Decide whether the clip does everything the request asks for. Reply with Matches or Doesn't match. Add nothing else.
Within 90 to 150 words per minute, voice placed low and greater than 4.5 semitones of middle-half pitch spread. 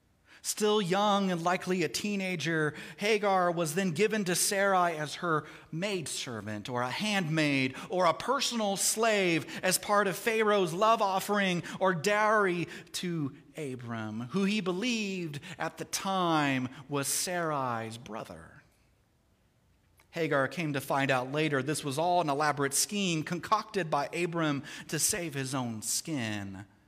Doesn't match